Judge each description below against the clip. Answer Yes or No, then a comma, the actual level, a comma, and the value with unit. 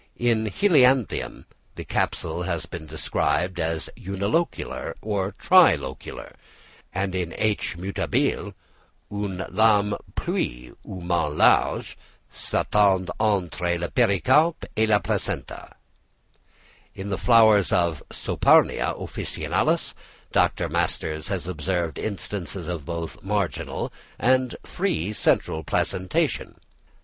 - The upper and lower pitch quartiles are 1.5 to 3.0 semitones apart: No, average, 3.7 semitones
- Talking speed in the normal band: No, slow, 105 wpm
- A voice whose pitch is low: Yes, very low, 95 Hz